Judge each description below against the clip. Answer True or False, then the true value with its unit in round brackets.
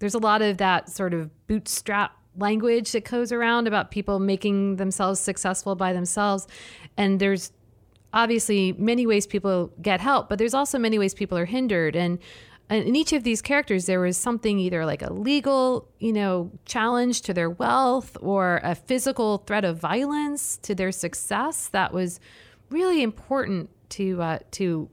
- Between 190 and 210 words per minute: False (170 wpm)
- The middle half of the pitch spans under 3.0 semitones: False (4.1 semitones)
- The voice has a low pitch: False (205 Hz)